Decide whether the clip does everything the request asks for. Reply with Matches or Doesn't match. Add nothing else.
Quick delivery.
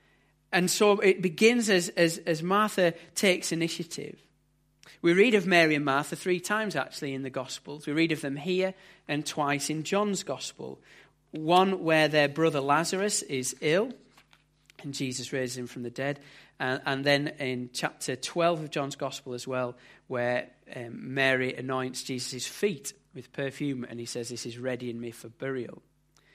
Doesn't match